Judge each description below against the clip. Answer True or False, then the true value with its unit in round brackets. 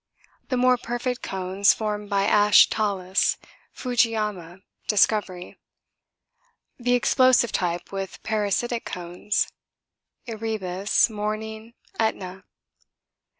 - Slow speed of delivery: True (85 wpm)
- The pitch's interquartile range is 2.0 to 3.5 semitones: True (3.0 semitones)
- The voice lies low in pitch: False (210 Hz)